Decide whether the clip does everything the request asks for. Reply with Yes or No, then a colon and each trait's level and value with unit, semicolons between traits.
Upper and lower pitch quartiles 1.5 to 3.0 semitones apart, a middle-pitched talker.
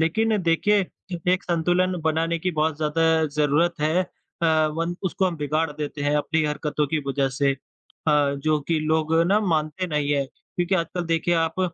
Yes: narrow, 2.5 semitones; medium, 160 Hz